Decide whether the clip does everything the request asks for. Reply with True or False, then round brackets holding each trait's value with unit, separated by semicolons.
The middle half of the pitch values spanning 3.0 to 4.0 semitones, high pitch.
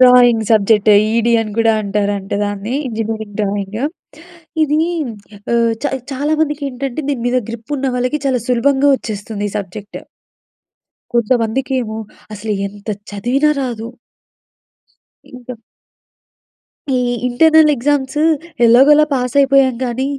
True (3.7 semitones; 240 Hz)